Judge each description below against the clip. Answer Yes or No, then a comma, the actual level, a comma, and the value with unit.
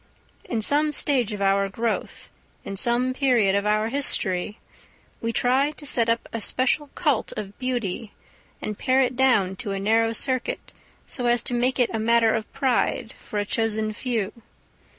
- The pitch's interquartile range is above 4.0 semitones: No, average, 3.3 semitones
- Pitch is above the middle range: Yes, high, 230 Hz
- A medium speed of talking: Yes, average, 170 wpm